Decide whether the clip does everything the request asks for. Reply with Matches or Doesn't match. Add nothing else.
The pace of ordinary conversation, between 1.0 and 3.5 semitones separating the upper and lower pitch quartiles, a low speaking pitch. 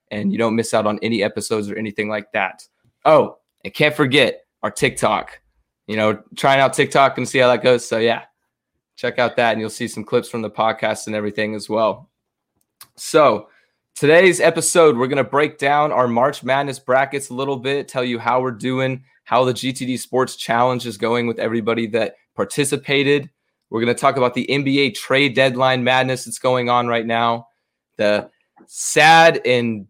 Matches